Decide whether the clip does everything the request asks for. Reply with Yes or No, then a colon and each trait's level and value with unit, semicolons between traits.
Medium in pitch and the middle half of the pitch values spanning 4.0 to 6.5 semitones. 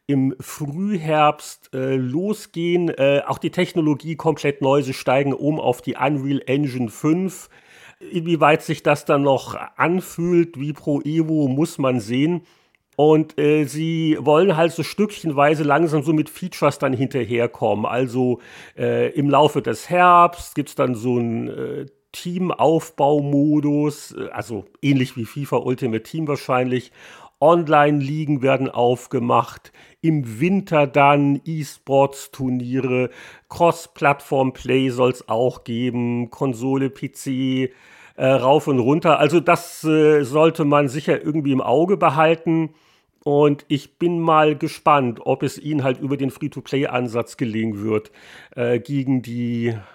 No: medium, 145 Hz; average, 3.3 semitones